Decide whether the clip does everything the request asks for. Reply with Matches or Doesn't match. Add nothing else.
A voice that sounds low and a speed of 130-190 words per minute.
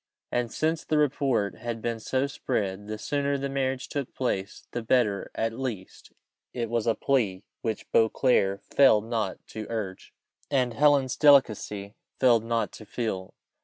Matches